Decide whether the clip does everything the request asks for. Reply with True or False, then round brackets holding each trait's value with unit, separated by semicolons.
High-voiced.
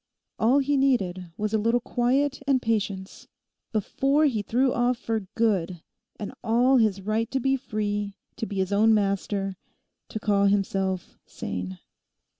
True (215 Hz)